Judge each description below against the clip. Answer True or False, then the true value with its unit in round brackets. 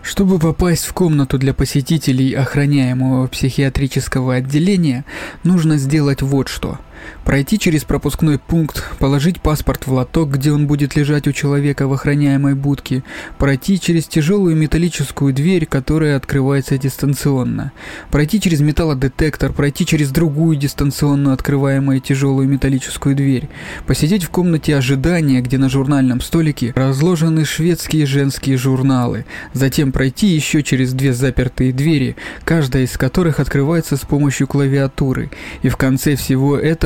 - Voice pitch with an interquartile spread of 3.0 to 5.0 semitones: False (2.5 semitones)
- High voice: False (140 Hz)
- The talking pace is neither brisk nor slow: True (130 wpm)